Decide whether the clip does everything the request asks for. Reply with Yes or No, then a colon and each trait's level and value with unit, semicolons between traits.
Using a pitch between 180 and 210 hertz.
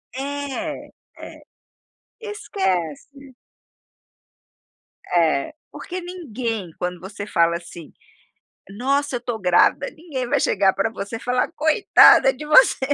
No: high, 245 Hz